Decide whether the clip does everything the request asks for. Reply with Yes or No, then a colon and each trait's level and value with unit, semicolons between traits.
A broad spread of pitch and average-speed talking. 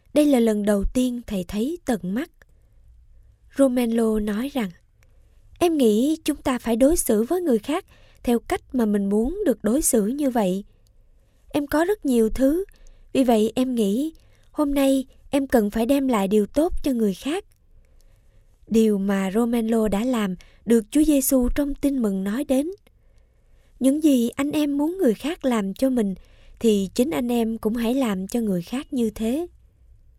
No: average, 4.3 semitones; average, 175 wpm